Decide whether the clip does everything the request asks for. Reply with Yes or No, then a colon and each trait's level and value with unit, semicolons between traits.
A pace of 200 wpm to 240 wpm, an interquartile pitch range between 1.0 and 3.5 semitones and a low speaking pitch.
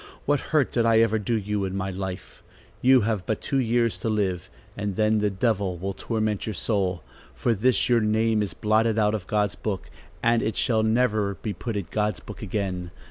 Yes: fast, 205 wpm; narrow, 2.5 semitones; low, 105 Hz